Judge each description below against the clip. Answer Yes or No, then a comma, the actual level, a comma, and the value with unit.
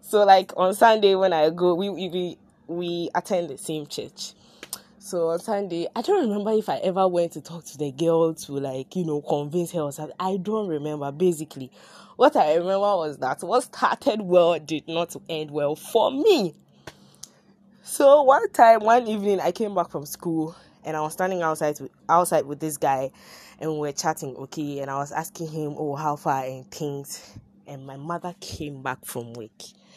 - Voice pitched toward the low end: No, medium, 170 Hz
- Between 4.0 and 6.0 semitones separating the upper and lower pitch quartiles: Yes, average, 4.4 semitones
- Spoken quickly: No, average, 195 wpm